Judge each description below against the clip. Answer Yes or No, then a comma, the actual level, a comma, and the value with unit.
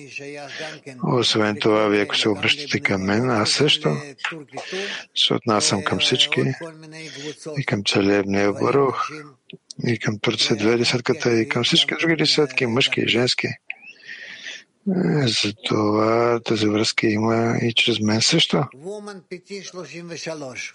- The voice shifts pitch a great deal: Yes, wide, 5.9 semitones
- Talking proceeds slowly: Yes, slow, 115 wpm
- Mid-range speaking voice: No, low, 125 Hz